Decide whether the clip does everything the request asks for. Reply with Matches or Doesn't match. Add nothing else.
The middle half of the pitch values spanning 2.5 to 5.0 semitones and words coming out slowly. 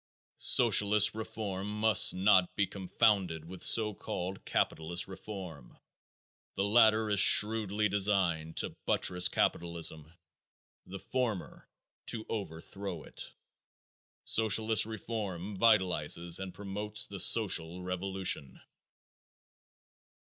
Matches